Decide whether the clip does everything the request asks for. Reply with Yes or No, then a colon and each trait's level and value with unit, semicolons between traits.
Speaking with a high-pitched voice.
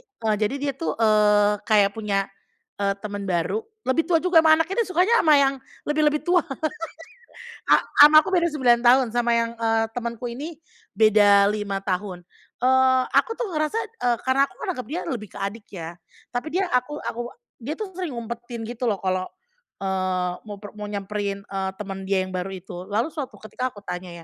Yes: high, 225 Hz